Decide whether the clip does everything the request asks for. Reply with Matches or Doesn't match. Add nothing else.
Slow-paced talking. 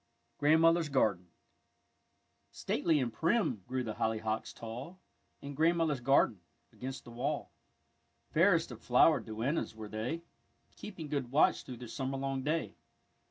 Matches